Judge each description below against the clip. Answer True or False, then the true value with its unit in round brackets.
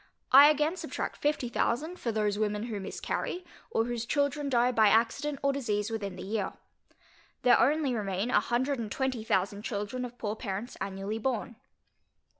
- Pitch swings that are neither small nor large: True (4.5 semitones)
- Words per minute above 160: True (170 wpm)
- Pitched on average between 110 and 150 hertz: False (235 Hz)